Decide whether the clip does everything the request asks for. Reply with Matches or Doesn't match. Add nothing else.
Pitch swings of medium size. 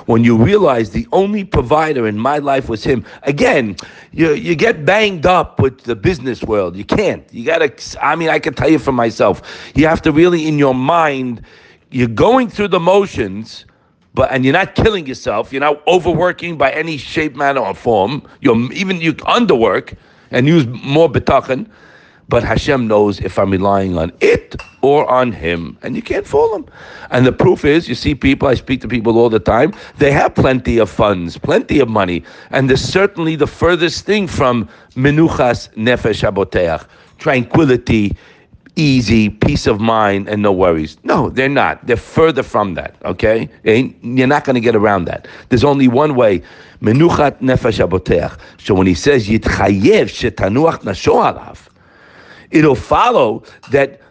Doesn't match